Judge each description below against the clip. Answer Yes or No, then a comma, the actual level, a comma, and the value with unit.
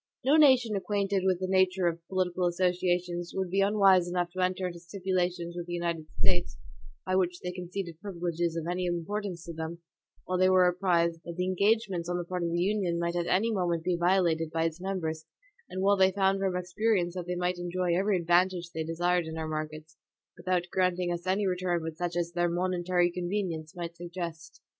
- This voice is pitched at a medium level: Yes, medium, 180 Hz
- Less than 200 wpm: No, fast, 205 wpm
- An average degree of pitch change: No, narrow, 1.5 semitones